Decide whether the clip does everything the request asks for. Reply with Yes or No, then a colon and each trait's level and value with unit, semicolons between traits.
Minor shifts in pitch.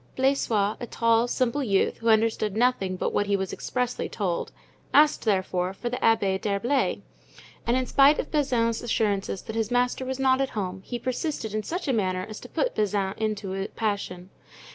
No: average, 4.1 semitones